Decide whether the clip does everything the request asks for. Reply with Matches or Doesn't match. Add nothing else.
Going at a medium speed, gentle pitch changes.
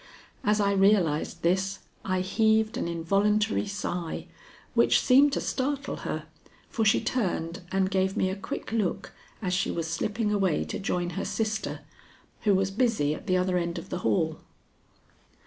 Doesn't match